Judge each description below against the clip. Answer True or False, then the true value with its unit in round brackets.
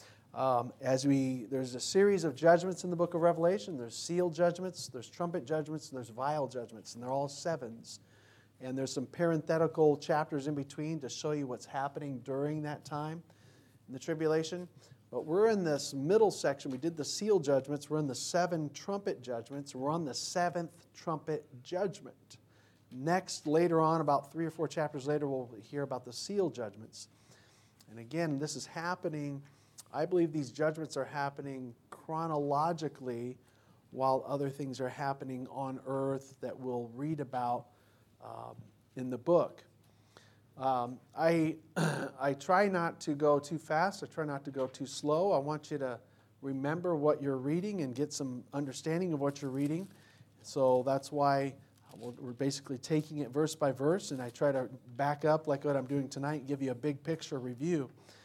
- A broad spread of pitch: False (3.5 semitones)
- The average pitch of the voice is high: False (140 Hz)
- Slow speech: False (175 wpm)